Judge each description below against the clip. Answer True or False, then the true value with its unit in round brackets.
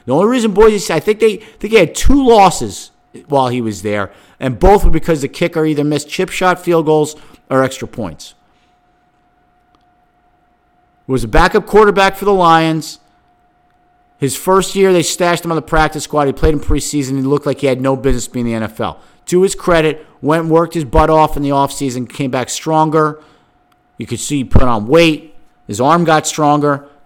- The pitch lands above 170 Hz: False (155 Hz)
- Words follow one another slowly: False (200 wpm)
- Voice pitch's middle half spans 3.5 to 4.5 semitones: True (3.9 semitones)